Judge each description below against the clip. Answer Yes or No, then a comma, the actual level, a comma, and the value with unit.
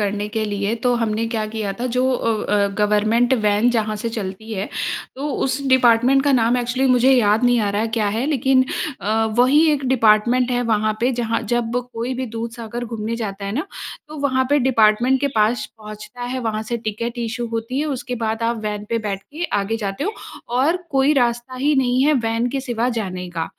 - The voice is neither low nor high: No, high, 235 Hz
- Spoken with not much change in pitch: No, average, 3.0 semitones